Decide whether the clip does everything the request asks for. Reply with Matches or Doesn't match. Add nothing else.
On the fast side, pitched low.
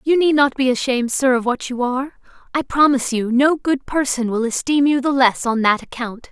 Doesn't match